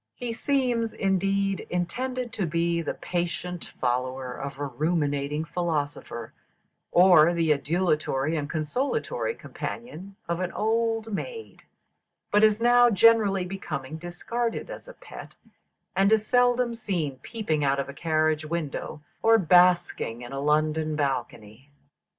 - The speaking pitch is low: No, medium, 175 Hz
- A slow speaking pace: Yes, slow, 130 wpm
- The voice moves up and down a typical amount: No, wide, 6.6 semitones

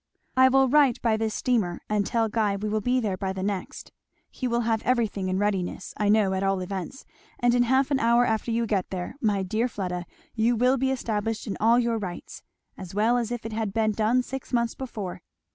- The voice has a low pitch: No, high, 220 Hz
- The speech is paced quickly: Yes, fast, 225 wpm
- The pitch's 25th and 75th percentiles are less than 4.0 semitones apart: Yes, average, 3.4 semitones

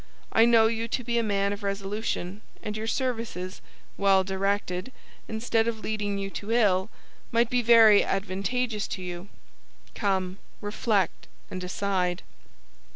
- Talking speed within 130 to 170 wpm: Yes, average, 140 wpm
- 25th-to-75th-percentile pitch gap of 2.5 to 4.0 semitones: Yes, average, 2.9 semitones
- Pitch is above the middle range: Yes, high, 205 Hz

